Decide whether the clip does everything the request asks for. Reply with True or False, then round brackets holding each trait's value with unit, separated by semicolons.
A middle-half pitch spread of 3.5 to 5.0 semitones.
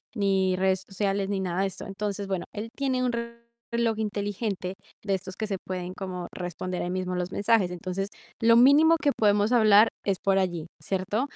False (2.6 semitones)